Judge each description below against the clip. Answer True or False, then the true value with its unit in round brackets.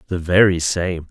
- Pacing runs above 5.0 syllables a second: False (4.4 syllables/s)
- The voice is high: False (90 Hz)